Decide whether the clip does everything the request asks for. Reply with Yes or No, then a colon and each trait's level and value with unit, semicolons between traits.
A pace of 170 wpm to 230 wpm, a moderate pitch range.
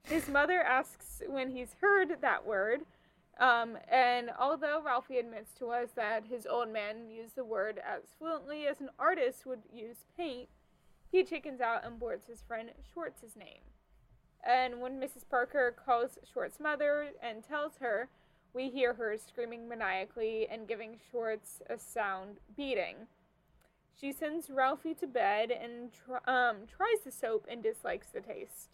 No: average, 155 wpm; average, 4.5 semitones